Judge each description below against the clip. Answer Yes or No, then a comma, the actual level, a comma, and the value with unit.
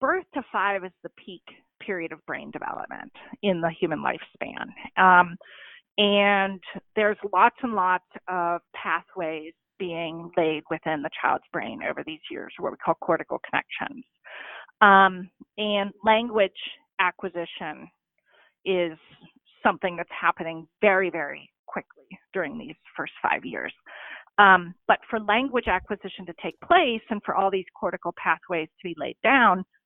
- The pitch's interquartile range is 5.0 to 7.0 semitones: No, average, 3.7 semitones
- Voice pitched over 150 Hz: Yes, high, 190 Hz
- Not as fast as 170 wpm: Yes, average, 140 wpm